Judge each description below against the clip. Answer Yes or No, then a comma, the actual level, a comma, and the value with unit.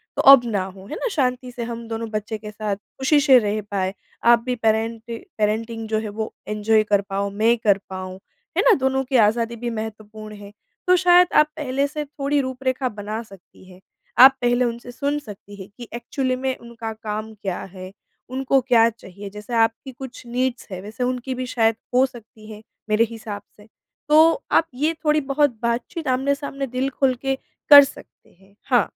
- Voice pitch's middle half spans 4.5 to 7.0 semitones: No, average, 3.7 semitones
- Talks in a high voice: Yes, high, 235 Hz